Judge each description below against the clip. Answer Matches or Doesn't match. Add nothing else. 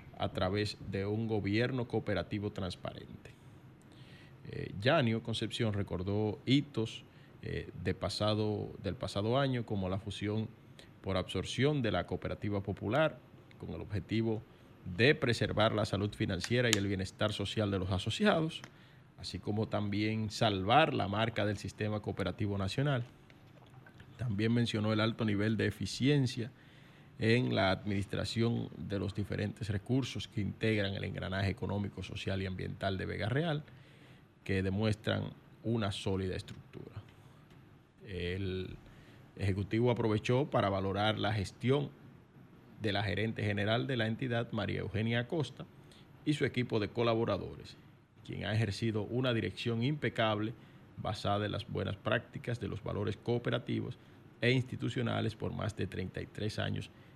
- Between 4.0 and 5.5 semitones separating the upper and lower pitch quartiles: Doesn't match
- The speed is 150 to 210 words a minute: Doesn't match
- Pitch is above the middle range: Doesn't match